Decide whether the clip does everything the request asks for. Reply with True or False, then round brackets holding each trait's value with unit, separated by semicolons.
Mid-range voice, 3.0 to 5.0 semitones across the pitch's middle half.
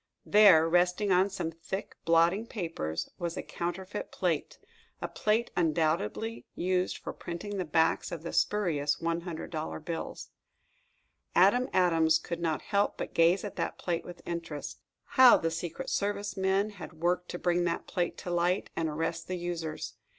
False (175 Hz; 2.6 semitones)